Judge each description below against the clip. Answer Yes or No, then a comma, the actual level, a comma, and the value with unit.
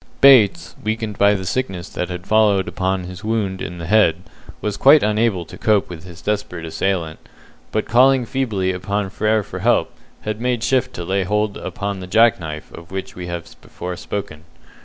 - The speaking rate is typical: Yes, average, 185 wpm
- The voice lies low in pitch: Yes, low, 100 Hz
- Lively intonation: No, average, 3.3 semitones